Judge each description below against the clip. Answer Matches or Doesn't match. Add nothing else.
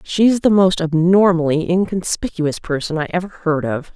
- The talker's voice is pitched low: Doesn't match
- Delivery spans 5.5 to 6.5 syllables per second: Doesn't match